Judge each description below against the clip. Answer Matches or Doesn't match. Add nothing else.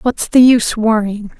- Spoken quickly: Doesn't match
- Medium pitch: Doesn't match